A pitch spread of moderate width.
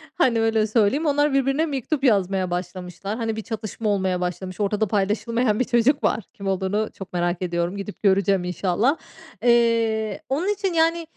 Yes: average, 4.9 semitones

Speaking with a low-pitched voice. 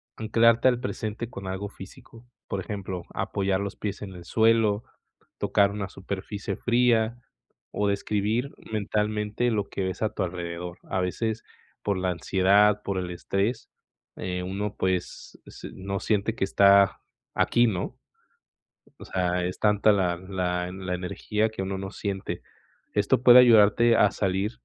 Yes: low, 100 Hz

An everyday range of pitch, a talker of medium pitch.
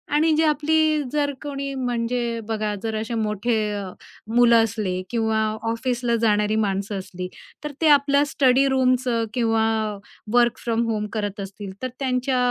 No: average, 3.7 semitones; high, 235 Hz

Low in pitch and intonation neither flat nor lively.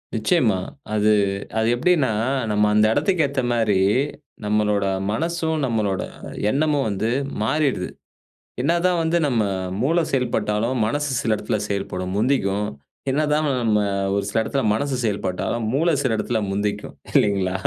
No: low, 115 Hz; wide, 5.8 semitones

